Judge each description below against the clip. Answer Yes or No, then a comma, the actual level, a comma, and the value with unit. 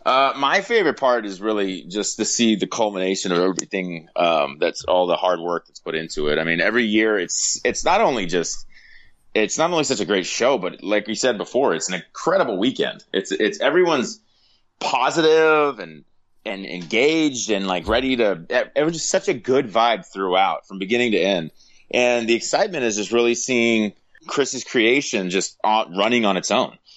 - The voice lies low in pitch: Yes, low, 110 Hz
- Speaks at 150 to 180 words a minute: No, average, 190 wpm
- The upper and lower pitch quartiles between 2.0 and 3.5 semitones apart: No, average, 4.3 semitones